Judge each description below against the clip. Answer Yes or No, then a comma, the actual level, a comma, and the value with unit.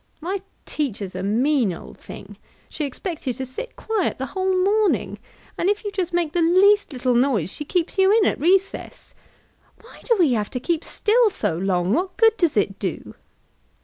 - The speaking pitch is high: Yes, very high, 330 Hz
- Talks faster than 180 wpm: Yes, average, 190 wpm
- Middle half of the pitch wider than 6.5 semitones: Yes, wide, 7.8 semitones